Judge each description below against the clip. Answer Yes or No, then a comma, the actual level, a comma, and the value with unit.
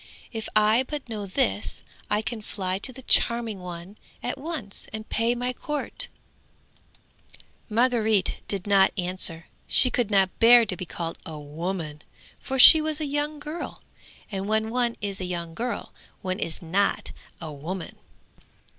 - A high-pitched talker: Yes, high, 210 Hz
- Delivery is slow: No, average, 155 wpm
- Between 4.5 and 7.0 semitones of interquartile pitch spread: Yes, average, 4.9 semitones